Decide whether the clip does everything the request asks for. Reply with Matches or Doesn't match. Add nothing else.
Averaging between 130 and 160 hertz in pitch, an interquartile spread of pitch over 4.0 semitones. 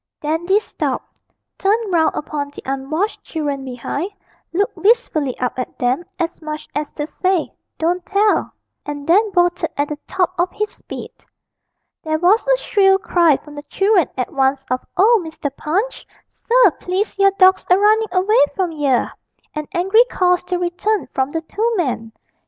Doesn't match